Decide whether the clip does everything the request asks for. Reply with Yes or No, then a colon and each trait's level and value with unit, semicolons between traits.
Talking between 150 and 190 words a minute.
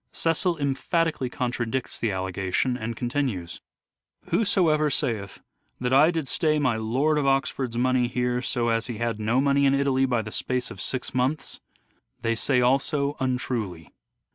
Yes: average, 165 wpm